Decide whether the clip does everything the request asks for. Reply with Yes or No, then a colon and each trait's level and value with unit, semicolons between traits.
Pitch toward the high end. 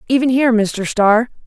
Yes: high, 235 Hz